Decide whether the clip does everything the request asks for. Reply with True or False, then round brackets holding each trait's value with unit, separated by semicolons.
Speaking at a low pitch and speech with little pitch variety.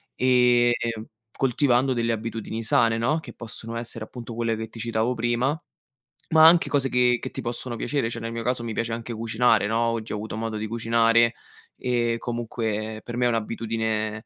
True (115 Hz; 1.4 semitones)